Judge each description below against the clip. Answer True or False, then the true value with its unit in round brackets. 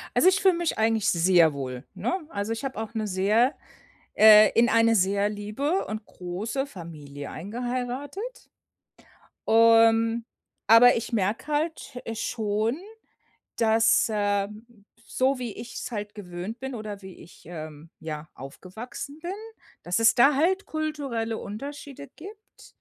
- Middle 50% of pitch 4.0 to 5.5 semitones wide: True (4.5 semitones)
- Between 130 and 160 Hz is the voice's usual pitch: False (225 Hz)